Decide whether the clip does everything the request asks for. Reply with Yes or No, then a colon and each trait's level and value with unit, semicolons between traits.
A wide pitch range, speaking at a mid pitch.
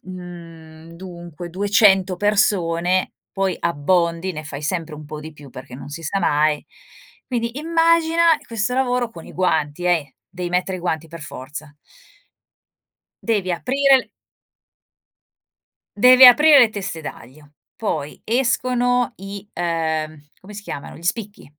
Yes: wide, 5.9 semitones; medium, 180 Hz